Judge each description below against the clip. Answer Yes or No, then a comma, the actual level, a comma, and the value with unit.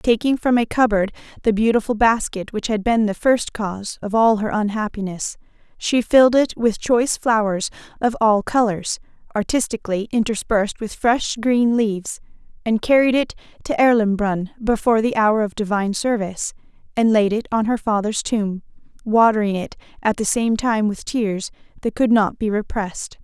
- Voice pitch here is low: No, high, 220 Hz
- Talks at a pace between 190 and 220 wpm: No, average, 165 wpm